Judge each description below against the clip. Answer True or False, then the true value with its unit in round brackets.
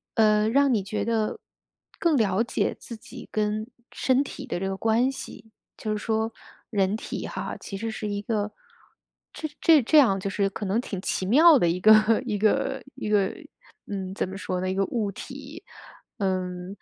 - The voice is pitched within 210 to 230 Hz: True (215 Hz)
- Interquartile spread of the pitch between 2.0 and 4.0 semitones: True (2.8 semitones)